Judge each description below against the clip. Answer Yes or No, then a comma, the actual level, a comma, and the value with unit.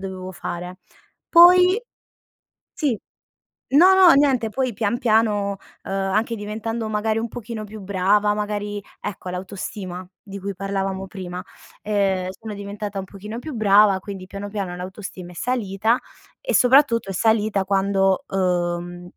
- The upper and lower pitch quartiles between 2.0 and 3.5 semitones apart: Yes, average, 2.8 semitones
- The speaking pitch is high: Yes, high, 205 Hz